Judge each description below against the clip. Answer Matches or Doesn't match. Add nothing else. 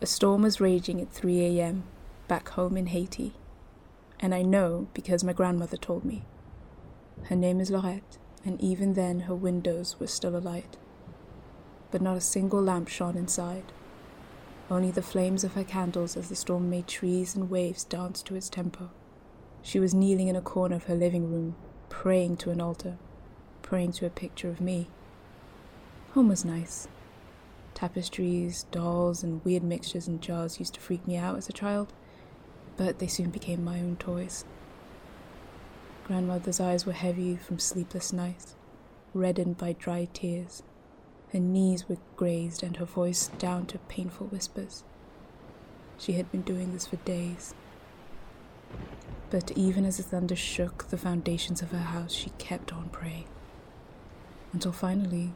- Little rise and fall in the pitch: Matches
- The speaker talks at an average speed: Matches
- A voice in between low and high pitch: Matches